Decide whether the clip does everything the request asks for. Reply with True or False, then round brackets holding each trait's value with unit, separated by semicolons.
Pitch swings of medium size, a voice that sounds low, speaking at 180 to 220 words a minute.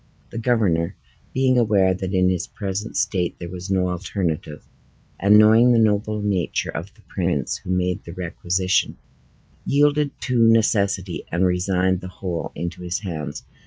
False (3.1 semitones; 95 Hz; 155 wpm)